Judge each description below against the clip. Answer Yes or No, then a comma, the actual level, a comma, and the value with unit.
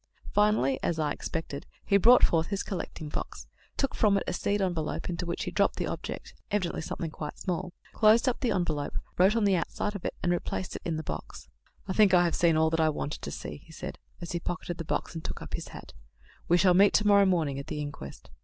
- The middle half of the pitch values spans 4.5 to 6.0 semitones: No, average, 3.9 semitones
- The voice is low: No, medium, 175 Hz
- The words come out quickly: Yes, fast, 240 wpm